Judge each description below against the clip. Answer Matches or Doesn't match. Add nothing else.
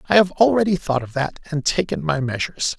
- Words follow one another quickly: Matches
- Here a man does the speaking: Matches